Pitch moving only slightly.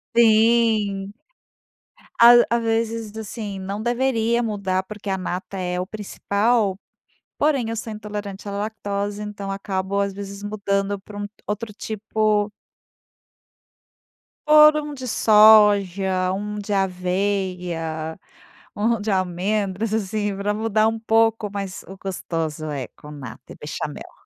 Yes: narrow, 2.3 semitones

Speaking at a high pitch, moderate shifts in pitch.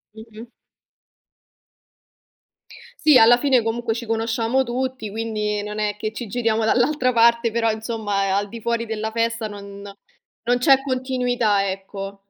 No: high, 225 Hz; narrow, 2.3 semitones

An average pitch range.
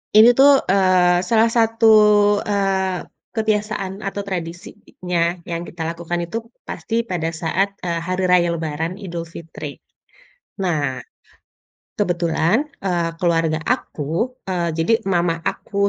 Yes: average, 3.1 semitones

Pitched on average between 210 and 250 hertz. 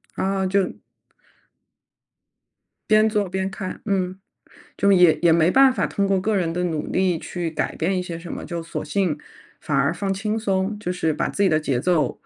No: medium, 185 Hz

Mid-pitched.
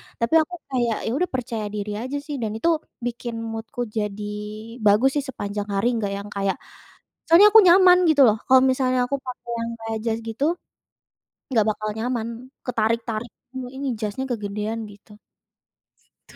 No: high, 230 Hz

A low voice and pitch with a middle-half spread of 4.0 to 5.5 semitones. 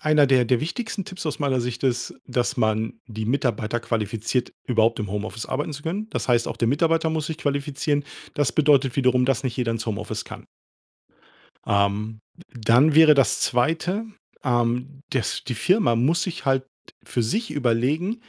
Yes: low, 130 Hz; average, 4.7 semitones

